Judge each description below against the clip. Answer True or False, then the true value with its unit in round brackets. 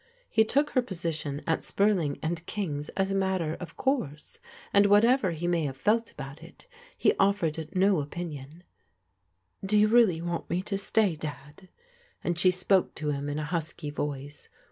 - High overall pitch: False (175 Hz)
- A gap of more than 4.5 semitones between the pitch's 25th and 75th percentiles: True (5.1 semitones)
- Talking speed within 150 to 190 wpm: True (185 wpm)